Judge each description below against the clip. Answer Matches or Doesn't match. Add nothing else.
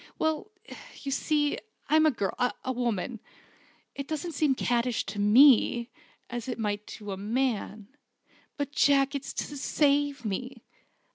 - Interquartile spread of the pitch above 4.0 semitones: Matches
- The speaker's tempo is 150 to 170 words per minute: Doesn't match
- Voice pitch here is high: Matches